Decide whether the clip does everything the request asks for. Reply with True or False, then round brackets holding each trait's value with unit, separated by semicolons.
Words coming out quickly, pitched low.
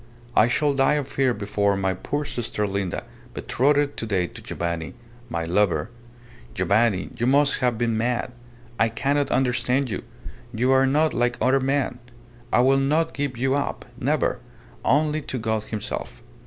False (160 wpm; 125 Hz)